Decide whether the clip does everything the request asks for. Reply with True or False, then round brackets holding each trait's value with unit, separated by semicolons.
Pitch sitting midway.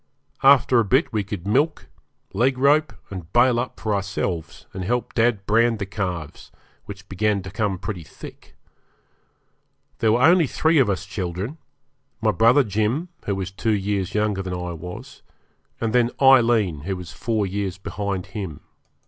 False (105 Hz)